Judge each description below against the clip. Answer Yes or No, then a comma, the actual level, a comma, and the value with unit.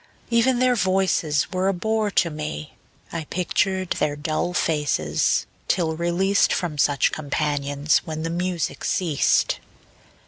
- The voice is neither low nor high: Yes, medium, 170 Hz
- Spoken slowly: Yes, slow, 130 wpm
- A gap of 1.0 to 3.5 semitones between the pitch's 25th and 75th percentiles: No, average, 4.1 semitones